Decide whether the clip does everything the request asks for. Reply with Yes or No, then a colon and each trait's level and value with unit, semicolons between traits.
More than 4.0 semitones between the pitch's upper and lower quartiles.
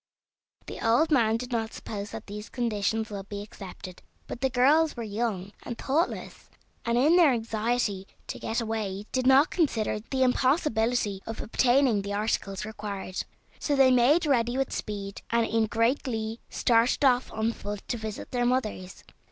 No: average, 3.4 semitones